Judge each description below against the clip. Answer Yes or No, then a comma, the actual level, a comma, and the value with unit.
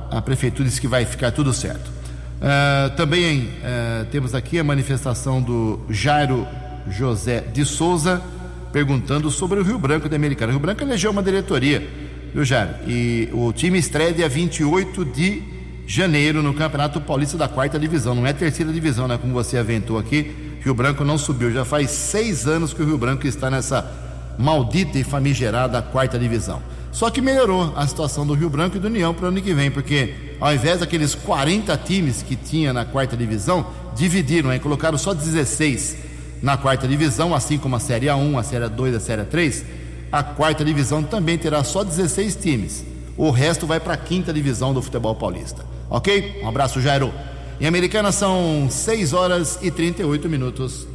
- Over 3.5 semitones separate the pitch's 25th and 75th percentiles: Yes, average, 4.9 semitones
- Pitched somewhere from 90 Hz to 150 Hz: Yes, medium, 140 Hz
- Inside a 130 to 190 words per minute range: Yes, average, 180 wpm